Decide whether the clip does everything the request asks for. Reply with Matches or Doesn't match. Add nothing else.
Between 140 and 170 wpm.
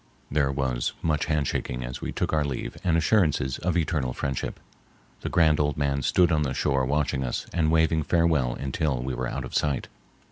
Doesn't match